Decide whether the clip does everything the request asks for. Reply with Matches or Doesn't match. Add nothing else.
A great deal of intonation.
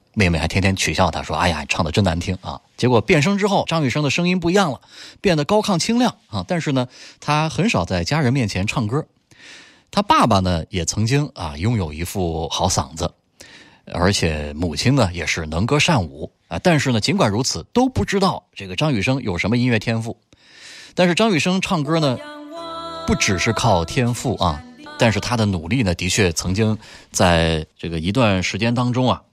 Matches